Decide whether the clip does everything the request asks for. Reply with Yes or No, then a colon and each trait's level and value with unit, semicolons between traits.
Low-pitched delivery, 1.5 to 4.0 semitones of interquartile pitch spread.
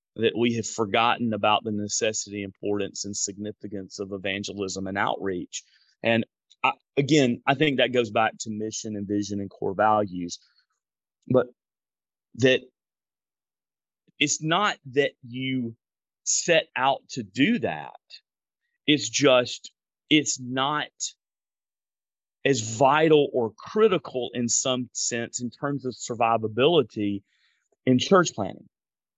No: low, 115 Hz; average, 4.9 semitones